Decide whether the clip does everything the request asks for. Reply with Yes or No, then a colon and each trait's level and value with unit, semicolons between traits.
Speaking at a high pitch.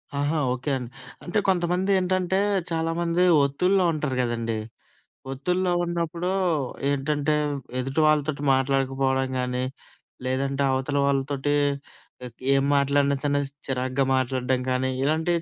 No: medium, 140 Hz